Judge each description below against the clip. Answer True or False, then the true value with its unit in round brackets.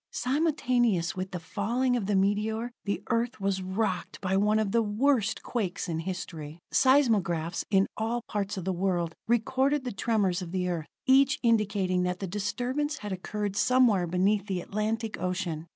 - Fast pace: False (170 wpm)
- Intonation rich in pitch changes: False (4.1 semitones)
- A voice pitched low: False (205 Hz)